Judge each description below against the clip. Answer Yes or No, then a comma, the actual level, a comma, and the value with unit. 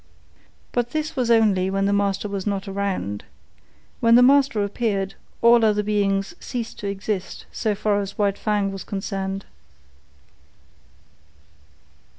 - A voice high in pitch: Yes, high, 205 Hz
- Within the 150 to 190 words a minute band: No, slow, 135 wpm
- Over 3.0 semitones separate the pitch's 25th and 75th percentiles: No, narrow, 2.5 semitones